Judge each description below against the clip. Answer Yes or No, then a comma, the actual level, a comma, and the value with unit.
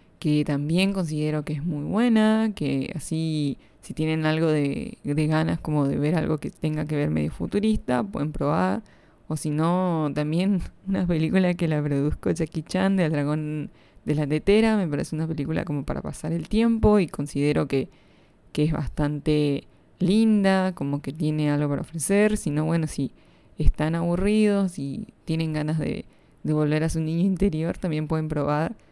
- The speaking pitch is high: No, medium, 155 Hz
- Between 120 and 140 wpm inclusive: No, average, 180 wpm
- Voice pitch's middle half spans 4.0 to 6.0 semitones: No, average, 3.5 semitones